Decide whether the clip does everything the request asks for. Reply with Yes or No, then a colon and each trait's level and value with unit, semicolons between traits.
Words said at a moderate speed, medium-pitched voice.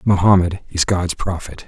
No: average, 145 wpm; very low, 90 Hz